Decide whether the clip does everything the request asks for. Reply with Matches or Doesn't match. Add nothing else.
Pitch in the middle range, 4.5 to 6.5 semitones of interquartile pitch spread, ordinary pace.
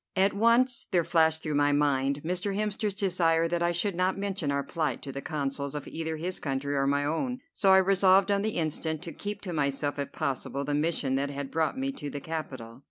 Doesn't match